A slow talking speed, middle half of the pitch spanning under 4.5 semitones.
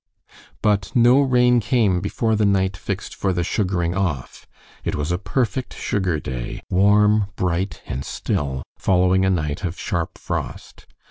No: average, 150 wpm; average, 3.2 semitones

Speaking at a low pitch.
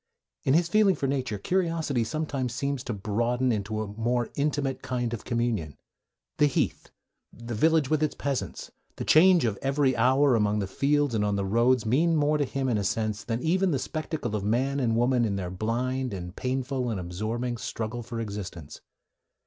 Yes: low, 125 Hz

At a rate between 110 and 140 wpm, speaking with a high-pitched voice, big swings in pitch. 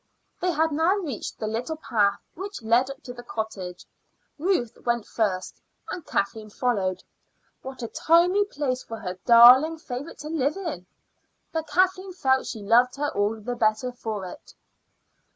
No: average, 160 wpm; very high, 250 Hz; wide, 6.5 semitones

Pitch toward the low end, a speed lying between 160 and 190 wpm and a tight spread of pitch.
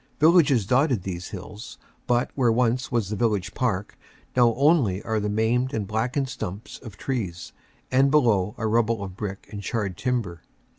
No: low, 115 Hz; average, 165 wpm; average, 3.9 semitones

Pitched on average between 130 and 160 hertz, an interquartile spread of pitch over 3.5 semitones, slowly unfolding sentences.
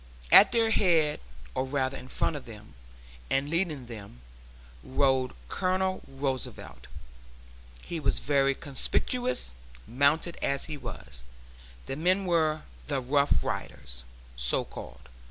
Yes: medium, 140 Hz; average, 4.5 semitones; slow, 120 wpm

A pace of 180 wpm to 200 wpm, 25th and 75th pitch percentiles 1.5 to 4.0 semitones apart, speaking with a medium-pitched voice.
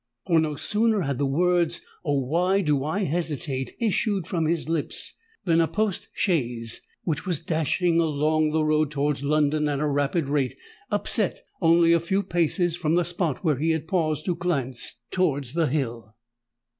No: average, 170 wpm; average, 3.4 semitones; medium, 160 Hz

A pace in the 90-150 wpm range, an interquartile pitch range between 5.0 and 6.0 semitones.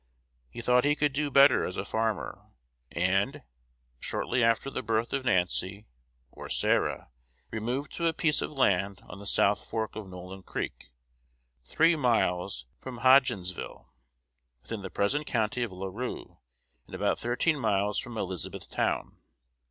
Yes: average, 145 wpm; average, 5.3 semitones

